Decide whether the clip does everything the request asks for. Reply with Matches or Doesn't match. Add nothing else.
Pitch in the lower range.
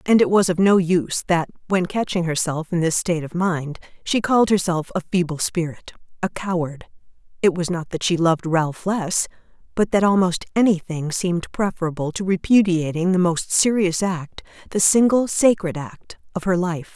Doesn't match